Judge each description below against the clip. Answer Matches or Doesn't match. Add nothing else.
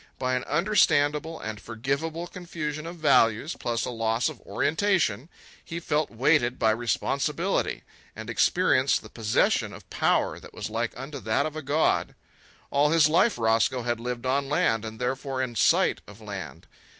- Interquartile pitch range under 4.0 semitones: Doesn't match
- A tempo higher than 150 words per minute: Matches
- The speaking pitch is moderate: Doesn't match